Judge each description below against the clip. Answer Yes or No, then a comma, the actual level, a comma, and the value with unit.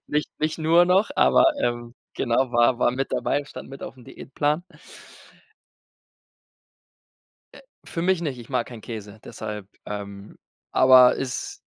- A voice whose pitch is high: No, low, 130 Hz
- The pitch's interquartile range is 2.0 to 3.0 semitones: No, average, 4.3 semitones